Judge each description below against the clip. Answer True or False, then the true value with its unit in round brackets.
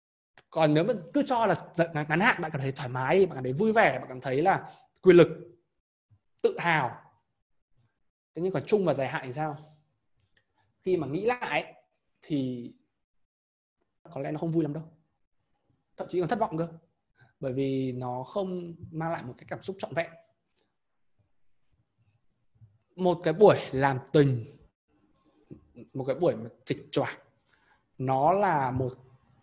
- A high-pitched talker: False (155 Hz)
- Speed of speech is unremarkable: False (160 wpm)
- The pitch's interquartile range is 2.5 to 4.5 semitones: False (5.4 semitones)